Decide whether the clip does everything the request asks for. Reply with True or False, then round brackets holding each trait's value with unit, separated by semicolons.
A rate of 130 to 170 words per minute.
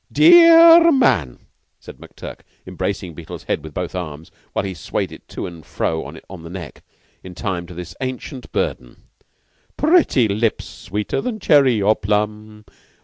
True (155 wpm)